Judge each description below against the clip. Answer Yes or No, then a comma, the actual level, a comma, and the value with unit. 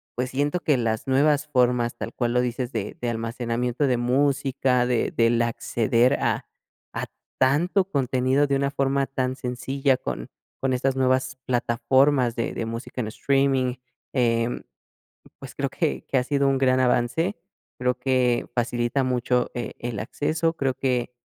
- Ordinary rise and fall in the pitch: No, narrow, 2.2 semitones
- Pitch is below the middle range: Yes, low, 130 Hz